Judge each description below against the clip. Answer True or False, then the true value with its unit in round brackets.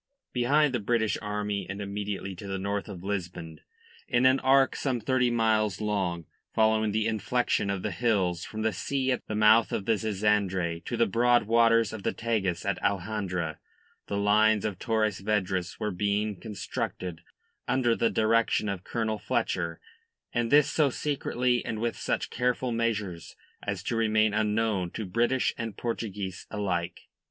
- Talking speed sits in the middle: True (165 wpm)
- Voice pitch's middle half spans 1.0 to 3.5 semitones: True (2.9 semitones)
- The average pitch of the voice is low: True (105 Hz)